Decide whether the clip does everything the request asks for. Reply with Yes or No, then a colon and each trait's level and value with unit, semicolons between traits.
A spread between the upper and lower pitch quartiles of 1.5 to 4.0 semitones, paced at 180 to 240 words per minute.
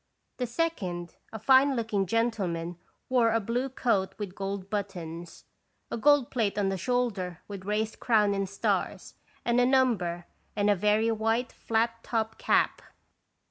No: average, 3.5 semitones; average, 155 wpm